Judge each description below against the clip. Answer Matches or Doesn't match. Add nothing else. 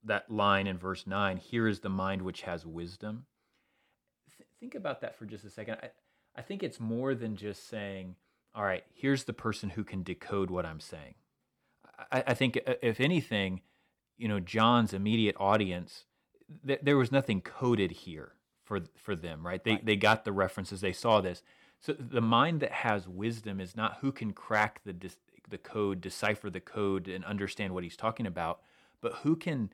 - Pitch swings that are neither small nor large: Matches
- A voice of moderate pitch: Doesn't match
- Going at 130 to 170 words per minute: Doesn't match